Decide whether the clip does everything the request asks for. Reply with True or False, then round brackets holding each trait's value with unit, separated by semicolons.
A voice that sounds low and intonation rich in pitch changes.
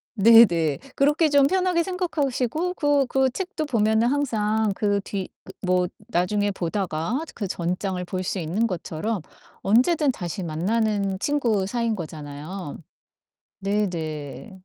False (210 Hz; 6.1 semitones)